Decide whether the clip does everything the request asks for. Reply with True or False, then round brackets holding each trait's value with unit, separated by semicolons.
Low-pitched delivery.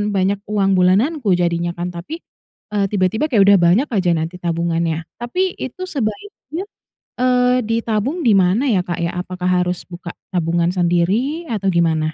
False (185 Hz)